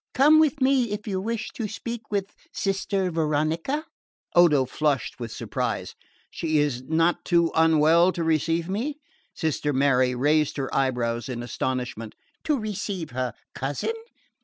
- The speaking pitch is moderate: Yes, medium, 165 Hz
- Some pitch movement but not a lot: No, wide, 6.9 semitones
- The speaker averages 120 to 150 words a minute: Yes, average, 140 wpm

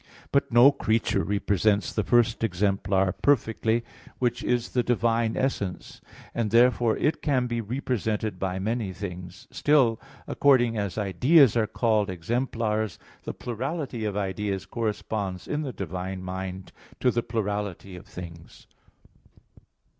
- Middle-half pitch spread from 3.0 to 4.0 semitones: Yes, average, 3.7 semitones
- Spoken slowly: Yes, slow, 130 wpm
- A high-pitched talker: No, low, 110 Hz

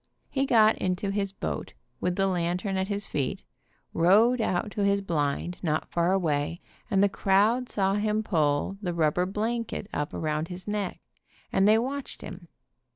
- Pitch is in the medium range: No, high, 195 Hz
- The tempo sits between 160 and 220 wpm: Yes, average, 165 wpm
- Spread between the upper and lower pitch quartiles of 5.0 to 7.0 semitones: No, average, 3.6 semitones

